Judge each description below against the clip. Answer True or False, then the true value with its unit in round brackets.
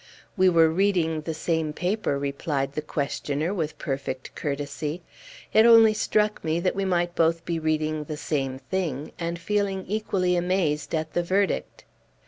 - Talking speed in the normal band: True (155 wpm)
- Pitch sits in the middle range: True (165 Hz)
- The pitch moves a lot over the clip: False (3.8 semitones)